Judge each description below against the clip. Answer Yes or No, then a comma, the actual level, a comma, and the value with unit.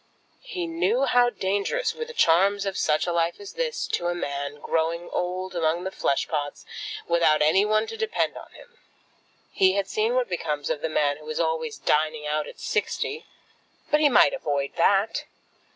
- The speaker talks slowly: No, average, 185 wpm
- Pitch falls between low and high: Yes, medium, 180 Hz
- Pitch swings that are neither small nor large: No, wide, 7.7 semitones